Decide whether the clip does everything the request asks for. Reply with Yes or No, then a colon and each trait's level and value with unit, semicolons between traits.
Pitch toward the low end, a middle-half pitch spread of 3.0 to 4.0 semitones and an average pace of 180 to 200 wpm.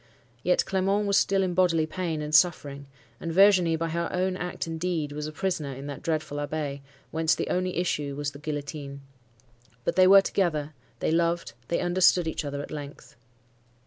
No: medium, 165 Hz; average, 3.6 semitones; average, 185 wpm